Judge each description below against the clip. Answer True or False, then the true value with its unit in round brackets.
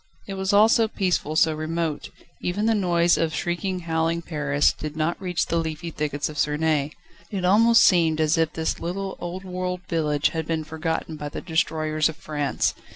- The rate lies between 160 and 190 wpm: True (185 wpm)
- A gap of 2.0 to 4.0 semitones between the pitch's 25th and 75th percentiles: True (2.8 semitones)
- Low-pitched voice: False (165 Hz)